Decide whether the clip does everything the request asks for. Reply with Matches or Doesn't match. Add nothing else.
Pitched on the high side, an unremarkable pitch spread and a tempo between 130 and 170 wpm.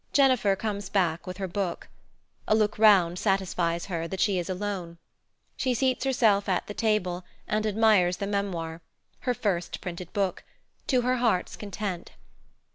Matches